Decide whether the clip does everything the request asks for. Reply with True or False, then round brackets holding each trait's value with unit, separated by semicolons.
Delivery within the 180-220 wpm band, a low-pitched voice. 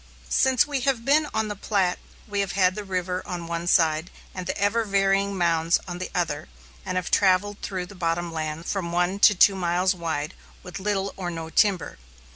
False (200 wpm; 185 Hz)